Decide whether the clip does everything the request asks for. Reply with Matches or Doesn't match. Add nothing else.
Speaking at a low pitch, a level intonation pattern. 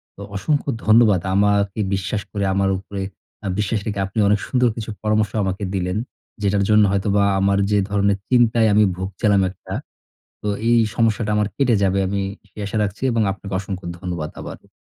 Matches